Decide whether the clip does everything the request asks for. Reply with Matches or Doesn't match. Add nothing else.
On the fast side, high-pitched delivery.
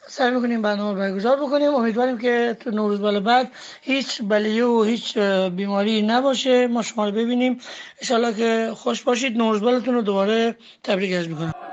Matches